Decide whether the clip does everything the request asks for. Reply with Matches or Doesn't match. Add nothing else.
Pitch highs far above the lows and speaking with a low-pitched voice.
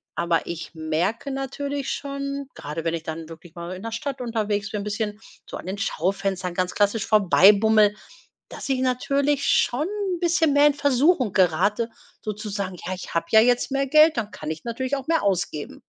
Doesn't match